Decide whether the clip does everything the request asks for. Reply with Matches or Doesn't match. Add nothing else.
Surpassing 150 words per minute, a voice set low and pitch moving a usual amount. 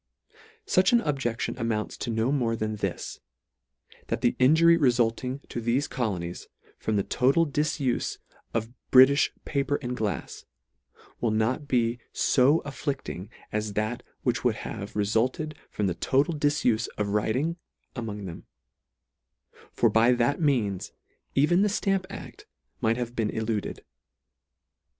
Doesn't match